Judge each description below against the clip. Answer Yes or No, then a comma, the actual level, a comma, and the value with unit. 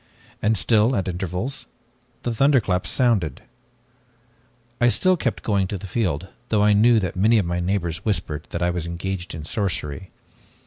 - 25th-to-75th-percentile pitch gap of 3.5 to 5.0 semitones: Yes, average, 4.4 semitones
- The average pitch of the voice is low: Yes, very low, 95 Hz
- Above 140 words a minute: Yes, average, 165 wpm